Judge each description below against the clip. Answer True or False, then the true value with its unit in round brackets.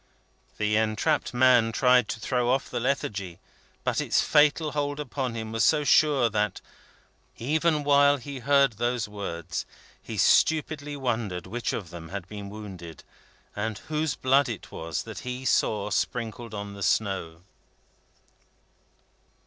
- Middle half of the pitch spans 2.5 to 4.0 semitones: False (5.3 semitones)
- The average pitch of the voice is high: False (120 Hz)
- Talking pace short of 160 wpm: True (140 wpm)